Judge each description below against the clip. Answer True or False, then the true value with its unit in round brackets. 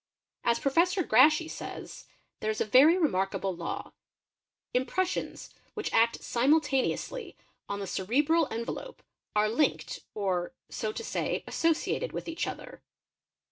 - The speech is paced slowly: True (125 wpm)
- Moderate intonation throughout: False (7.4 semitones)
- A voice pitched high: True (260 Hz)